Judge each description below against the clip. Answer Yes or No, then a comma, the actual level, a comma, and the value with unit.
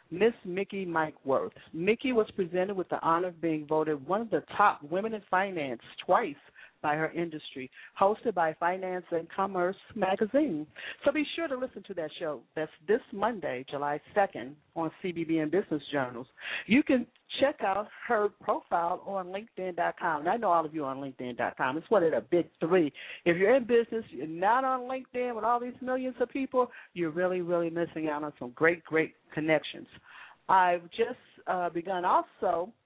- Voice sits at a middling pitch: Yes, medium, 180 Hz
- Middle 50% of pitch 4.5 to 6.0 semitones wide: Yes, wide, 5.5 semitones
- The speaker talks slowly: No, average, 175 wpm